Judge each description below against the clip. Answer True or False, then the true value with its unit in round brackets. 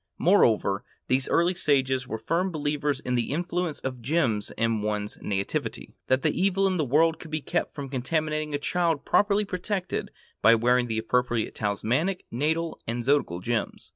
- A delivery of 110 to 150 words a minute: False (165 wpm)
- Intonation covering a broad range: True (5.9 semitones)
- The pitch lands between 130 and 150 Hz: True (140 Hz)